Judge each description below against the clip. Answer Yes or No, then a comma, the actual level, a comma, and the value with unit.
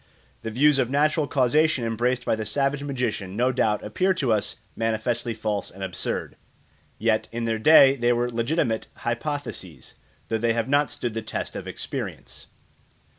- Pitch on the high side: No, low, 120 Hz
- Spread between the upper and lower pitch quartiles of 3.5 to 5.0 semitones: Yes, average, 3.8 semitones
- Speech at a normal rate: Yes, average, 165 wpm